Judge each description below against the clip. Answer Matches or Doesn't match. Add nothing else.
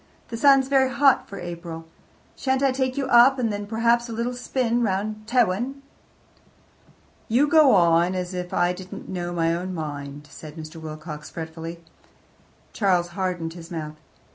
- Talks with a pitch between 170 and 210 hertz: Matches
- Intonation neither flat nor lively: Doesn't match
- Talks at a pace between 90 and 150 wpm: Doesn't match